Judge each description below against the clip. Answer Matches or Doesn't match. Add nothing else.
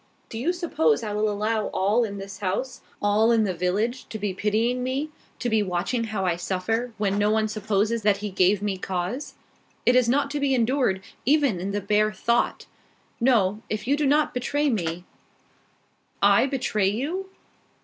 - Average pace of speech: Matches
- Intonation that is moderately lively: Matches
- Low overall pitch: Doesn't match